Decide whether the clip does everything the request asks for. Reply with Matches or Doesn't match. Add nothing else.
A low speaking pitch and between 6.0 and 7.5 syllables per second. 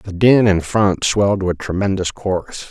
Doesn't match